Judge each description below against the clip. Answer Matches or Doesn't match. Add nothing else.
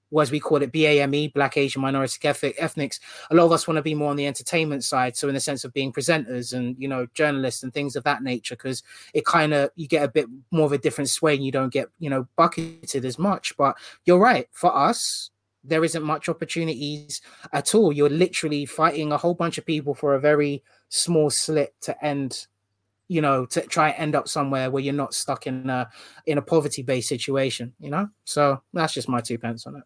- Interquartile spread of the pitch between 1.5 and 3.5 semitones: Matches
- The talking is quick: Matches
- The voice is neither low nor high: Matches